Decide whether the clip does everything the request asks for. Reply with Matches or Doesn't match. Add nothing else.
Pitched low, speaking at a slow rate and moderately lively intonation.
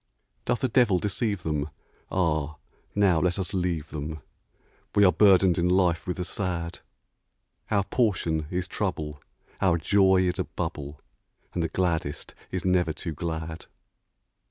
Doesn't match